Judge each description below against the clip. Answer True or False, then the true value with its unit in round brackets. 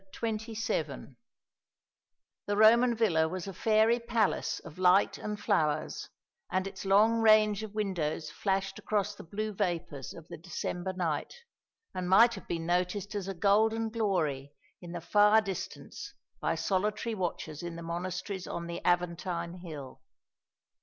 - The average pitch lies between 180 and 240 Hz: True (190 Hz)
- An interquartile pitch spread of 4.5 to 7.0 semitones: False (3.9 semitones)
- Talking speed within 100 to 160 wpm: True (145 wpm)